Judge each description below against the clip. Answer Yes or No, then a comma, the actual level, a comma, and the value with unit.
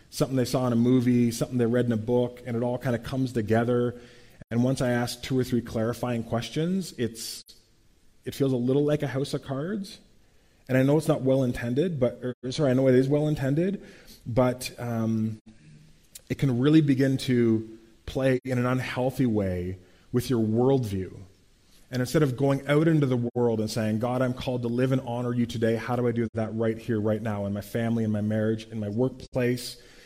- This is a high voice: No, low, 120 Hz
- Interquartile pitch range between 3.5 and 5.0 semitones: No, narrow, 2.6 semitones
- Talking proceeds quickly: Yes, fast, 210 wpm